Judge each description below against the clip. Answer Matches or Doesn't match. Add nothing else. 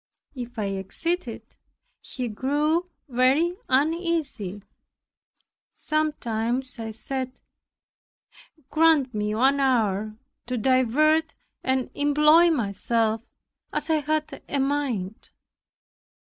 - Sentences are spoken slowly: Matches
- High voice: Matches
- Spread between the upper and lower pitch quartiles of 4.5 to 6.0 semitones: Matches